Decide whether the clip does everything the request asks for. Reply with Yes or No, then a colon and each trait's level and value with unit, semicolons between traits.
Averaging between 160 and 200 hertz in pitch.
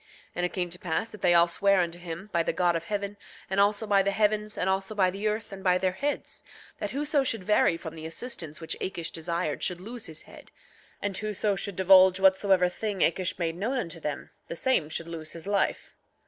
Yes: high, 190 Hz